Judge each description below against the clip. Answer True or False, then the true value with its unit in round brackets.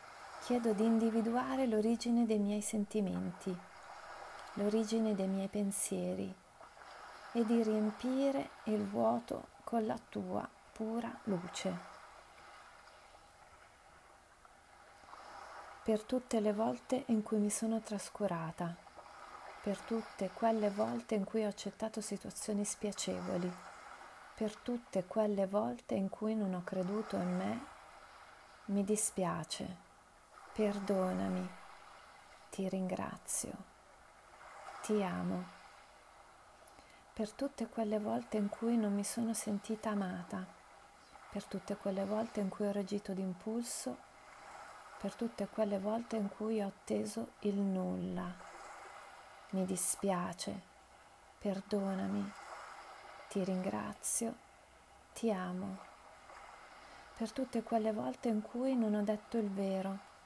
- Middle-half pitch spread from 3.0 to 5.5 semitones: False (2.6 semitones)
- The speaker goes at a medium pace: False (105 wpm)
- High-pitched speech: True (210 Hz)